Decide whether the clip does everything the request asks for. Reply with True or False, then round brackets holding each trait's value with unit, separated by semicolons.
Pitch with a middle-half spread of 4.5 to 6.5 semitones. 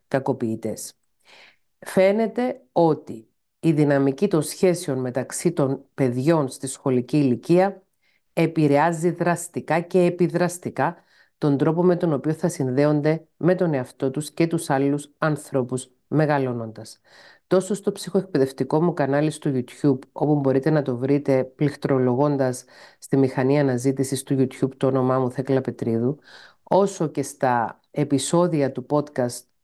False (4.0 semitones)